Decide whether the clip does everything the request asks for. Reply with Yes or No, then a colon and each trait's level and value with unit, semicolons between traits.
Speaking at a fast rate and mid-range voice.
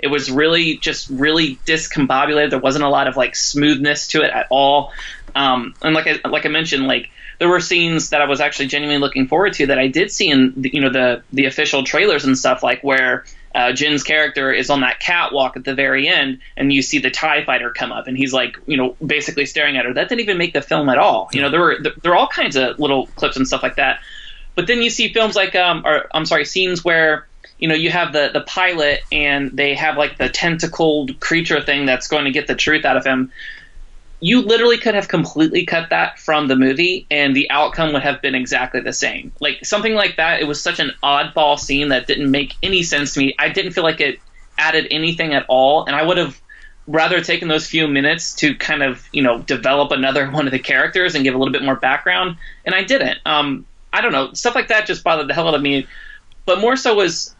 Yes: fast, 245 wpm; medium, 150 Hz